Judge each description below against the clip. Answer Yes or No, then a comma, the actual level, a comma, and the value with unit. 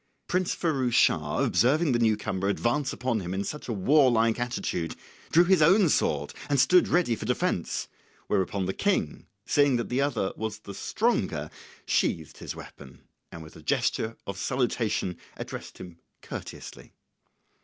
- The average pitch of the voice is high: No, low, 120 Hz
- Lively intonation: Yes, wide, 6.8 semitones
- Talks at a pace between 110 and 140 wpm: No, average, 155 wpm